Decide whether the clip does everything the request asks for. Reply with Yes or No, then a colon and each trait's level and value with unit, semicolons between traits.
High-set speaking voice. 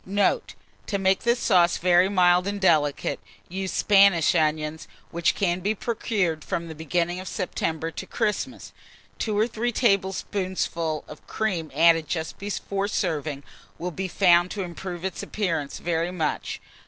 No: medium, 180 Hz